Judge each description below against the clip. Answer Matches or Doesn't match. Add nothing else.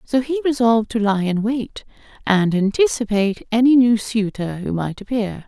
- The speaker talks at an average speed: Matches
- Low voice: Doesn't match